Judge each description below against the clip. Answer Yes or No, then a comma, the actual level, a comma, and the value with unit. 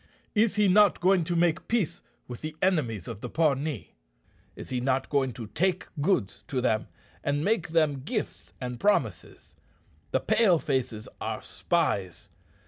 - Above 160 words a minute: No, average, 155 wpm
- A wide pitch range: Yes, wide, 6.9 semitones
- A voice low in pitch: No, medium, 150 Hz